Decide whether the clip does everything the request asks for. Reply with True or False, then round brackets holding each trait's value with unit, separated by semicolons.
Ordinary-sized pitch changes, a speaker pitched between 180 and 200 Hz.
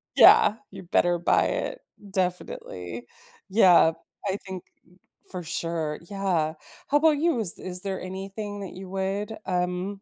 False (2.3 semitones; 190 Hz)